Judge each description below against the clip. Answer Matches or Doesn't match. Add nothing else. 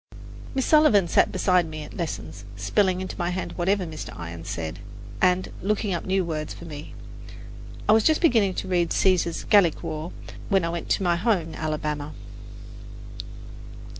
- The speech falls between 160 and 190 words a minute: Matches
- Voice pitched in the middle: Matches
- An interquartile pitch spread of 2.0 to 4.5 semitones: Matches